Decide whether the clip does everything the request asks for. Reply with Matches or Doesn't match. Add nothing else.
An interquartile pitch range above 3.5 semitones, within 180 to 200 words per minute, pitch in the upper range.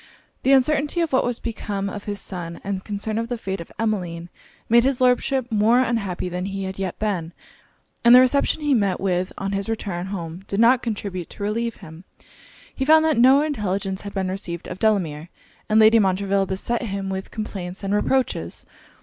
Matches